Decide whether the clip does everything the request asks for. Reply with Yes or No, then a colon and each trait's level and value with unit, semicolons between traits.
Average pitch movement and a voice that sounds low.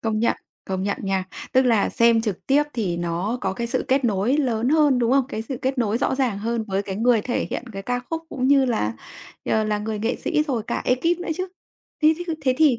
No: average, 4.2 semitones; high, 235 Hz